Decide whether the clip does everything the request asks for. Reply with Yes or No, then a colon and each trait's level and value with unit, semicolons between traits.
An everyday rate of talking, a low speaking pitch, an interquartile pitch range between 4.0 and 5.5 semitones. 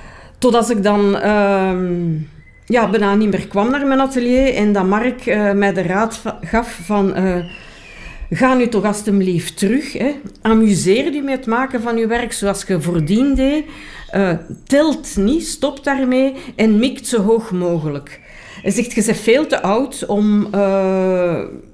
No: average, 165 wpm; high, 215 Hz; average, 4.4 semitones